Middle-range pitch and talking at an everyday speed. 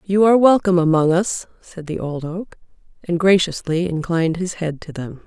Yes: medium, 175 Hz; average, 180 wpm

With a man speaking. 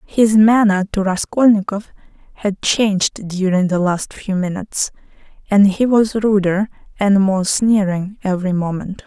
No: female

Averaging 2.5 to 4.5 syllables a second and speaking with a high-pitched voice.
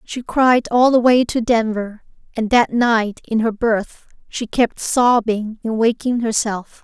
Yes: 3.7 syllables/s; high, 230 Hz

